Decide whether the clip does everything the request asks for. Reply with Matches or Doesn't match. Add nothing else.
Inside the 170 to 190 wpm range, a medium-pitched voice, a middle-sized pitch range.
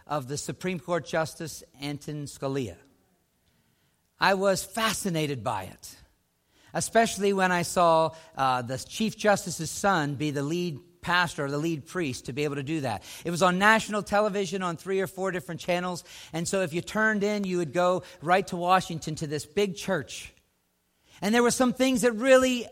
Matches